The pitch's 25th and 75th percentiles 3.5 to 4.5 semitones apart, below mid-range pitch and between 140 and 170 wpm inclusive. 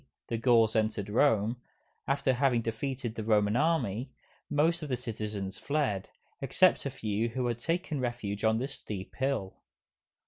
Yes: average, 4.1 semitones; low, 120 Hz; average, 150 wpm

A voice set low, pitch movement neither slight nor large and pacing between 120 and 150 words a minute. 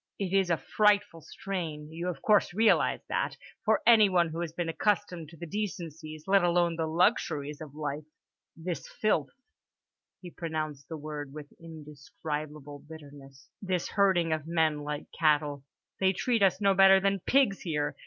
No: medium, 165 Hz; average, 4.3 semitones; average, 145 wpm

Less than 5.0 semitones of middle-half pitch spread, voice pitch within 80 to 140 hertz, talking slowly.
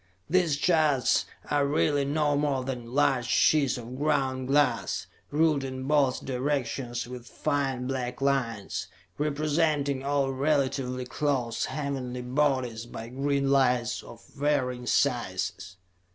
Yes: narrow, 2.5 semitones; low, 135 Hz; slow, 120 wpm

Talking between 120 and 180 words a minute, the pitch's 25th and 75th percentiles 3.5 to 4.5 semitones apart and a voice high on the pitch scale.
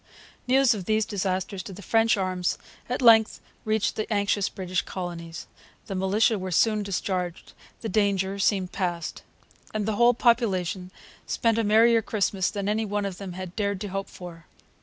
No: average, 170 wpm; average, 2.9 semitones; high, 200 Hz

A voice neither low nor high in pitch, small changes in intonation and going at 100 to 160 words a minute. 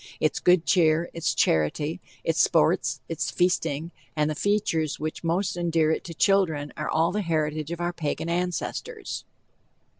Yes: medium, 165 Hz; narrow, 2.3 semitones; average, 155 wpm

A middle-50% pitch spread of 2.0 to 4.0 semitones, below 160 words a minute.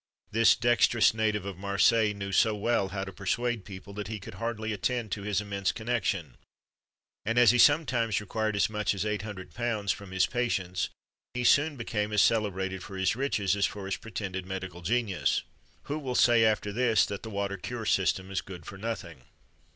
No: average, 3.1 semitones; average, 190 wpm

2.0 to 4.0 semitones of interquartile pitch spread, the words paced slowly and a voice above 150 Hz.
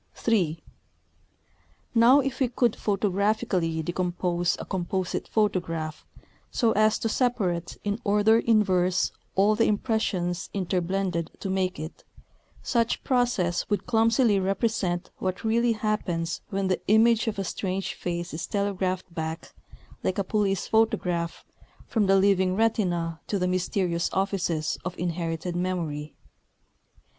Yes: average, 3.6 semitones; slow, 125 wpm; high, 190 Hz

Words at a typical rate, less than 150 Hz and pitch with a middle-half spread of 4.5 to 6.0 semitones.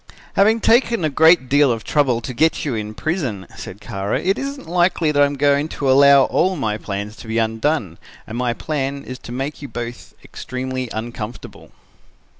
Yes: average, 185 wpm; low, 135 Hz; average, 5.2 semitones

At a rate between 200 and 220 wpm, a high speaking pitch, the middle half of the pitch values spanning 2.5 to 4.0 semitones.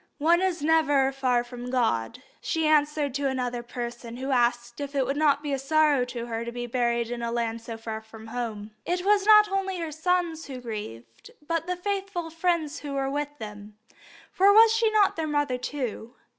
No: fast, 205 wpm; very high, 275 Hz; average, 5.3 semitones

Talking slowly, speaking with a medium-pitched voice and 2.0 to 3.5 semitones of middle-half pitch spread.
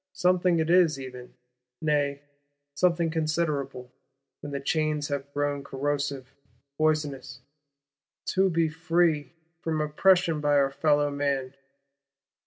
Yes: slow, 105 wpm; medium, 145 Hz; average, 2.7 semitones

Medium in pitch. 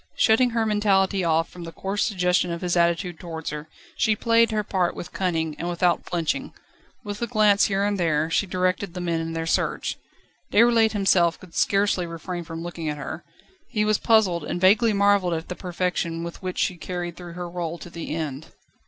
Yes: medium, 180 Hz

